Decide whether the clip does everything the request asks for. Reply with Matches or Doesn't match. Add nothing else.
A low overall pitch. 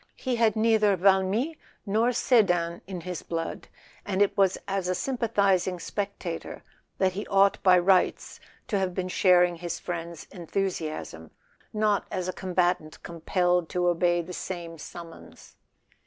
Doesn't match